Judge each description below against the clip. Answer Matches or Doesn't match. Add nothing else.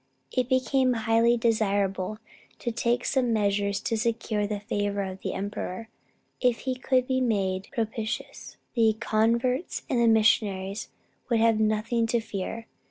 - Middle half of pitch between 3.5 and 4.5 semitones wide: Doesn't match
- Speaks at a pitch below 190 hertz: Doesn't match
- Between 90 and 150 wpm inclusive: Matches